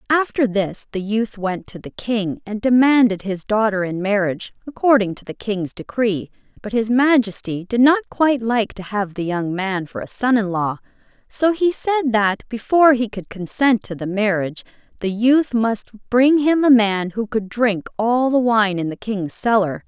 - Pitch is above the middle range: Yes, high, 220 Hz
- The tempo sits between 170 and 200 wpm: Yes, average, 195 wpm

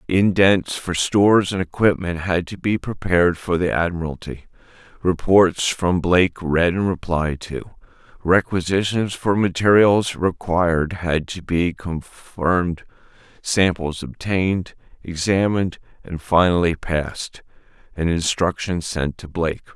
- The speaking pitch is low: Yes, very low, 90 Hz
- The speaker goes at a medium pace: No, slow, 115 wpm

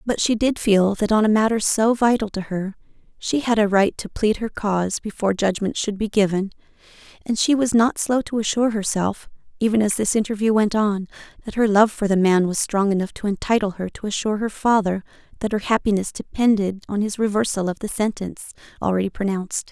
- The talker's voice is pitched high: Yes, high, 210 Hz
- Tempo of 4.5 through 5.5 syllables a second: No, 5.8 syllables/s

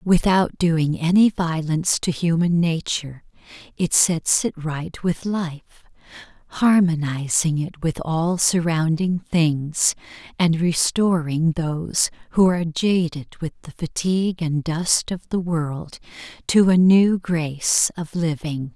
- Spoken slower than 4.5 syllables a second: Yes, 3.8 syllables/s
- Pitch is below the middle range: No, medium, 165 Hz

